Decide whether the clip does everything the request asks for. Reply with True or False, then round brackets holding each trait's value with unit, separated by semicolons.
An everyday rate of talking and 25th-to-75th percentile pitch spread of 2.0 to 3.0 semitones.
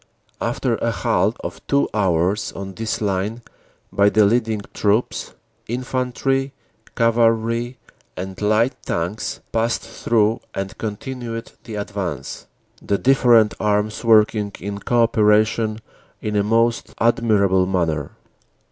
False (115 wpm; 2.5 semitones)